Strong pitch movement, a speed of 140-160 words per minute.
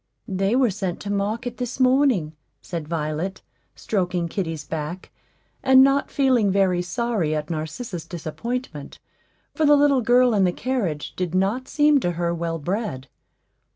Yes: wide, 6.8 semitones; average, 150 wpm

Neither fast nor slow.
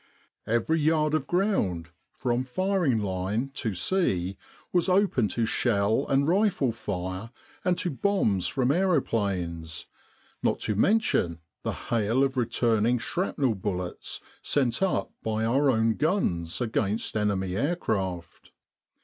No: slow, 125 wpm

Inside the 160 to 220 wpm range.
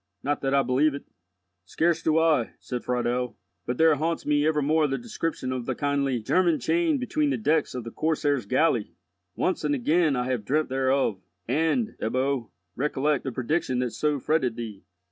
Yes: average, 180 wpm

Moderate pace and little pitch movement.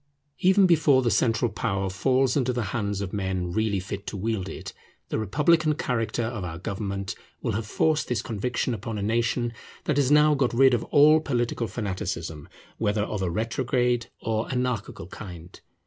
No: average, 175 wpm; average, 4.2 semitones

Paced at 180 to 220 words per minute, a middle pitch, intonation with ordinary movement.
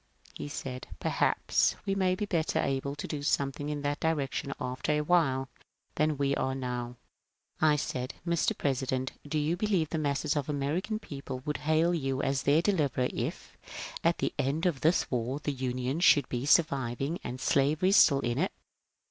Yes: average, 185 wpm; medium, 145 Hz; average, 3.1 semitones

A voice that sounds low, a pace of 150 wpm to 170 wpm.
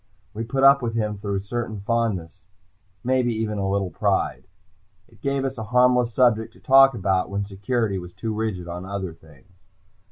No: low, 110 Hz; average, 185 wpm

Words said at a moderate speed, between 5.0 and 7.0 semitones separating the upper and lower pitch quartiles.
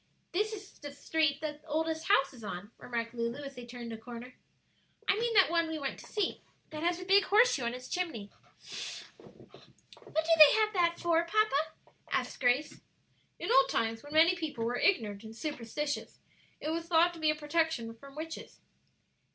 Yes: average, 190 wpm; wide, 5.5 semitones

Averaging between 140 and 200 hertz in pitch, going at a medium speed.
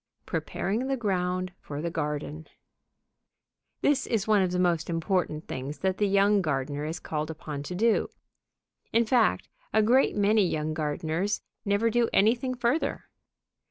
Yes: medium, 185 Hz; average, 150 wpm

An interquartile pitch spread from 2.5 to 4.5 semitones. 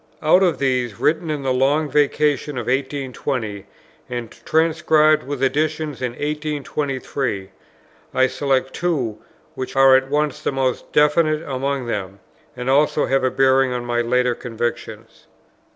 Yes: average, 3.0 semitones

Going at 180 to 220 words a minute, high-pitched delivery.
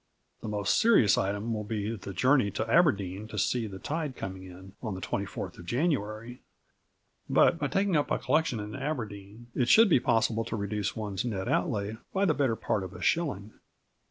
No: average, 190 wpm; low, 110 Hz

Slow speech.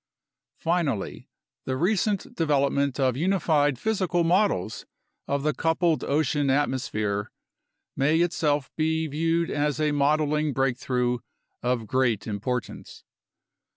Yes: slow, 110 wpm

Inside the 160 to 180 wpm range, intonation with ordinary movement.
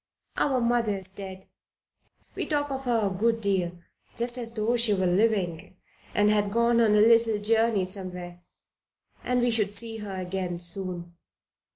Yes: average, 165 wpm; average, 3.6 semitones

